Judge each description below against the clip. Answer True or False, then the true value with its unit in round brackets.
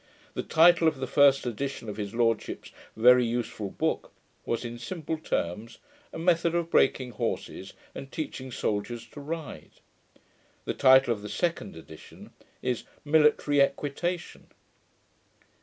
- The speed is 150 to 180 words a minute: False (135 wpm)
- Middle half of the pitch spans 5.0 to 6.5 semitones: True (5.3 semitones)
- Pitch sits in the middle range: False (130 Hz)